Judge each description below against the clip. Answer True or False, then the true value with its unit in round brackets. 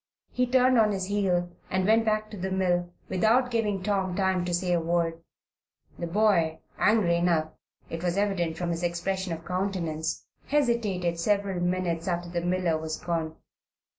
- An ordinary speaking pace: True (165 wpm)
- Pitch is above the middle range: False (180 Hz)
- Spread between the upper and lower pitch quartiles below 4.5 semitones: True (3.0 semitones)